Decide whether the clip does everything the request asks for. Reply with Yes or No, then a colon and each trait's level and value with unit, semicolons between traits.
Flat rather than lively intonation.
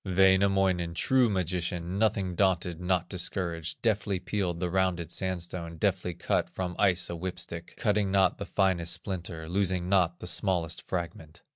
Yes: narrow, 1.9 semitones